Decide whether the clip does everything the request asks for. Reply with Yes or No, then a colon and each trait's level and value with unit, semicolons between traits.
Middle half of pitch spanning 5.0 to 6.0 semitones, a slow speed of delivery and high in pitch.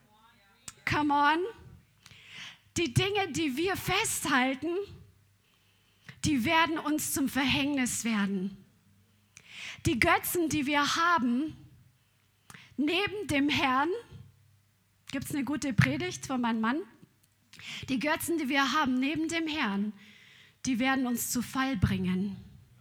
Yes: average, 5.3 semitones; slow, 115 wpm; very high, 275 Hz